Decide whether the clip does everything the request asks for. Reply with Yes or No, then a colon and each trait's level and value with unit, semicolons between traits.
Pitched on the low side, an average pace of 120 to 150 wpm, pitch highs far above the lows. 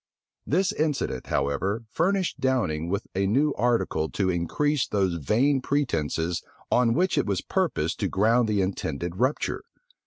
Yes: low, 110 Hz; average, 145 wpm; wide, 8.0 semitones